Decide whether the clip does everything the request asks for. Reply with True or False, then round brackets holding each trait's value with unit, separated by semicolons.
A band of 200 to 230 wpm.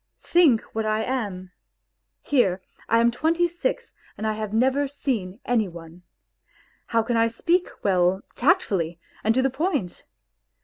False (145 wpm)